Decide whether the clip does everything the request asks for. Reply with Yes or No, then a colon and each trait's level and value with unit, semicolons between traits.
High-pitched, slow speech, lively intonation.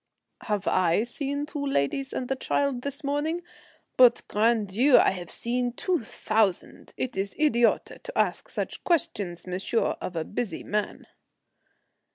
No: high, 240 Hz; average, 150 wpm; wide, 5.8 semitones